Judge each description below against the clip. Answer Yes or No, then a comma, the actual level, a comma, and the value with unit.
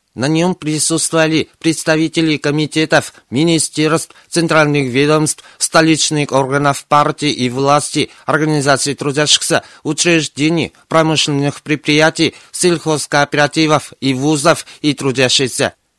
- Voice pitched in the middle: Yes, medium, 150 Hz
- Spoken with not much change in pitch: Yes, narrow, 1.9 semitones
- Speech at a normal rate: No, slow, 85 wpm